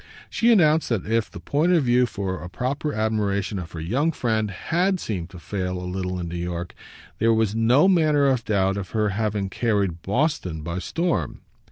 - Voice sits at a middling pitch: No, low, 105 Hz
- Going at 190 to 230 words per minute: Yes, average, 195 wpm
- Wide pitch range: Yes, wide, 6.6 semitones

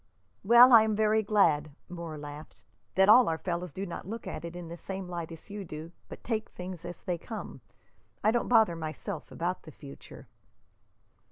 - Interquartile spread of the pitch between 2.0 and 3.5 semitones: No, average, 4.5 semitones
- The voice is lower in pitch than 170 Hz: No, medium, 180 Hz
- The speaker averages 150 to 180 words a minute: No, average, 190 wpm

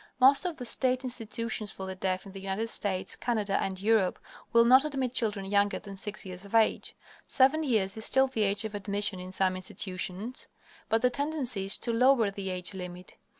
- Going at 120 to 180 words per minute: No, average, 200 wpm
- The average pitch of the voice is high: Yes, high, 210 Hz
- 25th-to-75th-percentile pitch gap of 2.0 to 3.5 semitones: No, average, 4.5 semitones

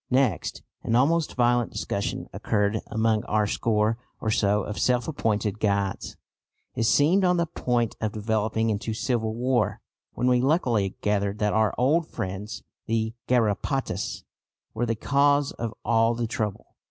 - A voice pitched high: No, low, 115 Hz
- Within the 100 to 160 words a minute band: Yes, average, 150 wpm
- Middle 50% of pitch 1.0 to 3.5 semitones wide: Yes, average, 2.9 semitones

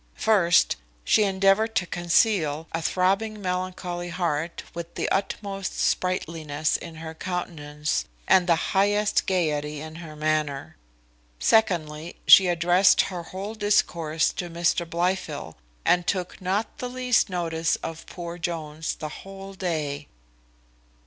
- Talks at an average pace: No, slow, 125 wpm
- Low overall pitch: No, medium, 175 Hz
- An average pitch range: Yes, average, 3.2 semitones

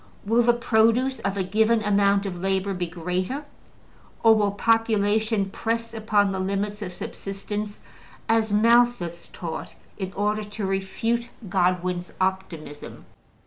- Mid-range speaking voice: No, high, 205 Hz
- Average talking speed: No, slow, 130 wpm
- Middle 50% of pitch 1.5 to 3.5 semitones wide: Yes, average, 2.9 semitones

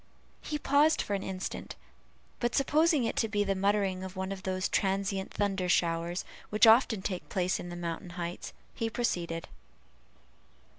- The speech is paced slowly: No, average, 160 wpm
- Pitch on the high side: Yes, high, 195 Hz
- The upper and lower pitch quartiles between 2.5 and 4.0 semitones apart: Yes, average, 3.3 semitones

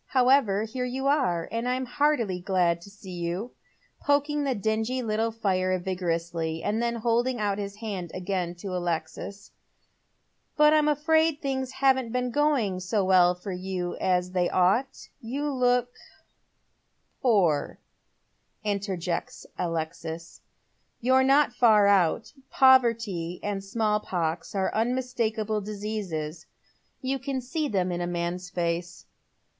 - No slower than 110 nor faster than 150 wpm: Yes, average, 140 wpm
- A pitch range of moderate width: No, wide, 5.8 semitones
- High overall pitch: Yes, high, 210 Hz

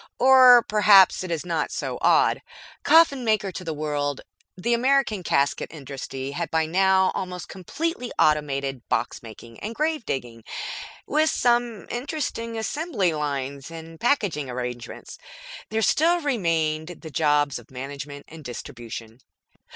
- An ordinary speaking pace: No, slow, 130 wpm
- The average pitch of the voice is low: No, medium, 165 Hz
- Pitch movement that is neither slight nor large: No, wide, 8.6 semitones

